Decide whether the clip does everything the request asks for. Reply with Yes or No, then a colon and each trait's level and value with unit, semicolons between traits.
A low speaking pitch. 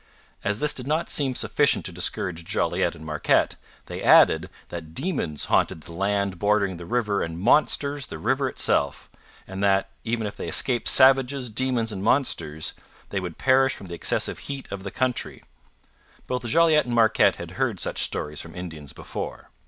Yes: low, 105 Hz